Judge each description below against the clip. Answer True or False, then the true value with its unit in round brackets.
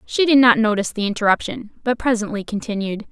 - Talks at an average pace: True (175 wpm)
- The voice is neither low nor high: False (220 Hz)